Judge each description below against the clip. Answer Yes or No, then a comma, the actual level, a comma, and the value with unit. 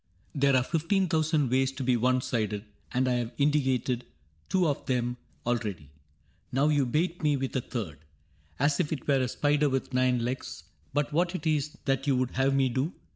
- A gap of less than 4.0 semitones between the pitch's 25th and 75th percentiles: Yes, average, 3.2 semitones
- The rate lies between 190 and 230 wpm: Yes, average, 200 wpm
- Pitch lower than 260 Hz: Yes, low, 135 Hz